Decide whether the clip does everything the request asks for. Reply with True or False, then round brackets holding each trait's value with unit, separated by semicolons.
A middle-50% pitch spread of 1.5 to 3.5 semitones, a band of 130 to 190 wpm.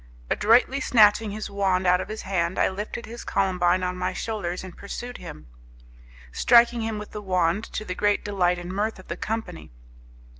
True (3.2 semitones; 185 wpm)